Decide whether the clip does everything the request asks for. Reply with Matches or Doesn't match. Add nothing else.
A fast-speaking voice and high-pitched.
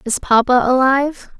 Doesn't match